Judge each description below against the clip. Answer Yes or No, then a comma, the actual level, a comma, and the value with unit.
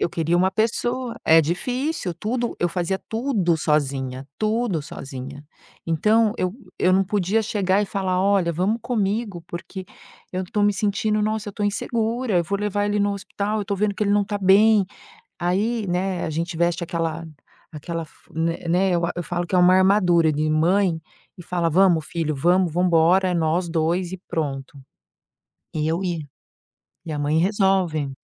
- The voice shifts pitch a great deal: No, average, 3.7 semitones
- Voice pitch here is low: No, medium, 185 Hz